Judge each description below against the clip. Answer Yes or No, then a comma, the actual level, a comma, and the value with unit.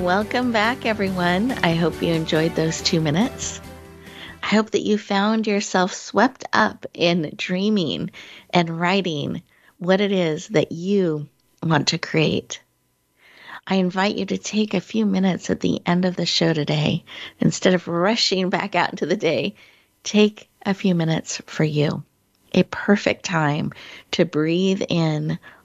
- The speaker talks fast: No, average, 150 wpm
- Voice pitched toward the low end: No, medium, 180 Hz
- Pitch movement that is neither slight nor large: Yes, average, 3.6 semitones